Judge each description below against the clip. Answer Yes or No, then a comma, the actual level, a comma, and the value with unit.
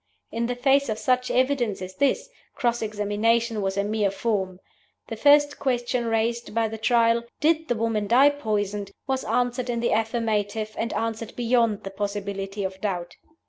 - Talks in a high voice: Yes, high, 225 Hz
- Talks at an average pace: Yes, average, 170 wpm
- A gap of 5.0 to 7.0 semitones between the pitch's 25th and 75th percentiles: No, average, 3.0 semitones